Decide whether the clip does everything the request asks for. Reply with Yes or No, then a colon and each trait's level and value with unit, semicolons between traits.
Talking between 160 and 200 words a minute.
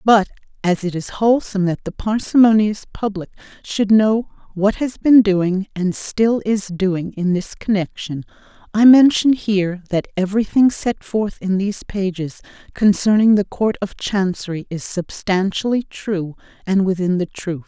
No: average, 150 wpm